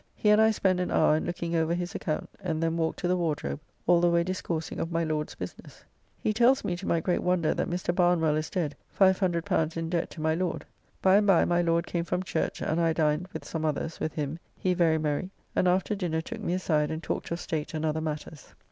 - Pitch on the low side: No, medium, 170 Hz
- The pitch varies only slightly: Yes, narrow, 2.3 semitones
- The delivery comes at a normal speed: No, fast, 240 wpm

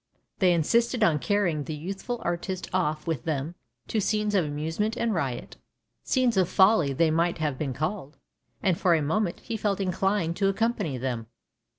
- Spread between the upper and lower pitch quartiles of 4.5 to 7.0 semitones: Yes, average, 5.3 semitones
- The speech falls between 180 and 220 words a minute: Yes, average, 185 wpm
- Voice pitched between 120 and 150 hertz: No, medium, 175 Hz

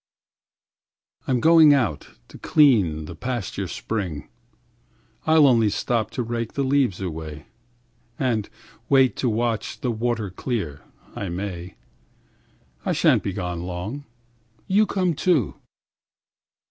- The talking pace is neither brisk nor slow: No, slow, 110 wpm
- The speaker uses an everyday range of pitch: No, wide, 6.3 semitones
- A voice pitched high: No, low, 115 Hz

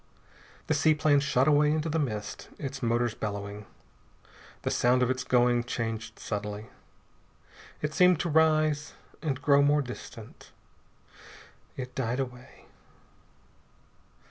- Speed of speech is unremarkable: No, slow, 115 wpm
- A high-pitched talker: No, low, 130 Hz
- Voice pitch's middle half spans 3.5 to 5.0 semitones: Yes, average, 4.2 semitones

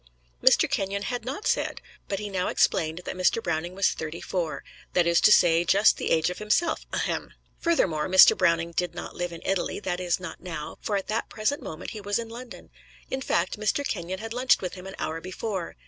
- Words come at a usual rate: No, fast, 215 wpm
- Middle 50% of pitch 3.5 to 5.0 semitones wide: Yes, average, 3.8 semitones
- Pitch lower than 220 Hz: Yes, medium, 185 Hz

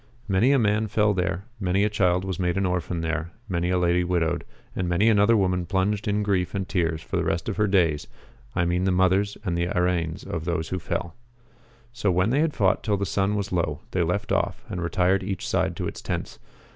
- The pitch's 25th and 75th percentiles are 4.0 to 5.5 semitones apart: No, average, 2.7 semitones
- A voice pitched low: Yes, very low, 90 Hz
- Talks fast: Yes, fast, 225 wpm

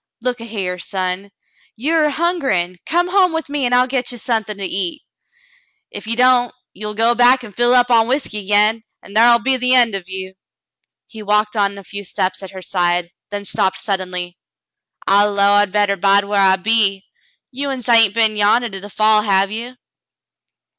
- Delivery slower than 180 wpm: No, average, 195 wpm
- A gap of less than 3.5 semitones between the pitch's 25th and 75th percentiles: No, average, 3.9 semitones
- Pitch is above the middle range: Yes, high, 210 Hz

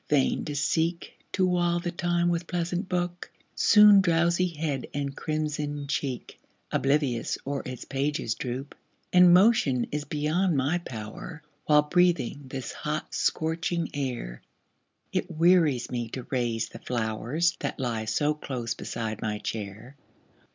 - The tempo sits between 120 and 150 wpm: Yes, slow, 135 wpm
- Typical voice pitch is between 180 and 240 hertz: No, medium, 150 Hz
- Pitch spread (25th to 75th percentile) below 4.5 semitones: No, average, 5.3 semitones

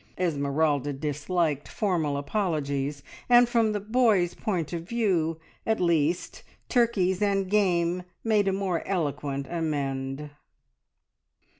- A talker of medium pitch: Yes, medium, 170 Hz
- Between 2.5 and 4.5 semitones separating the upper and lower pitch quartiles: No, wide, 5.5 semitones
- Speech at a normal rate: No, slow, 110 wpm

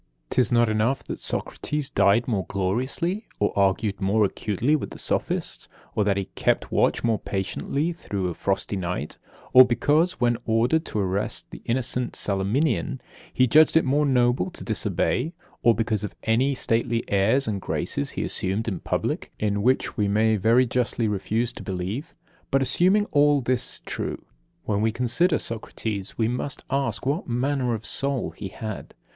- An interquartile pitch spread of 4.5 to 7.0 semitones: Yes, average, 4.8 semitones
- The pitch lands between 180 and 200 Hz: No, low, 115 Hz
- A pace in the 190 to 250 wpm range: No, average, 165 wpm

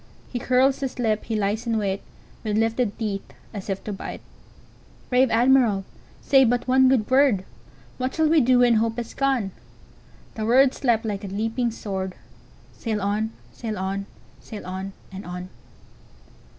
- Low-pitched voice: No, high, 225 Hz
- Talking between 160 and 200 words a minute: No, average, 145 wpm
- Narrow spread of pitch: No, average, 4.0 semitones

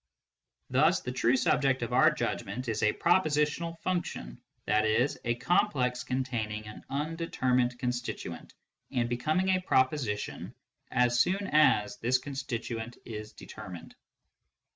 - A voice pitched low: Yes, low, 125 Hz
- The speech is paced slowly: Yes, slow, 120 wpm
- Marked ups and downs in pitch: No, average, 4.4 semitones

